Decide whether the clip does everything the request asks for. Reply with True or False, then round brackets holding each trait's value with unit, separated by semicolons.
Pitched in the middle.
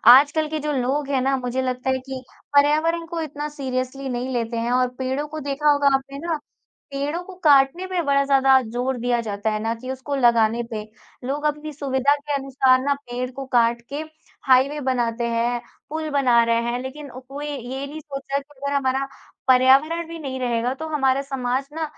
False (270 Hz)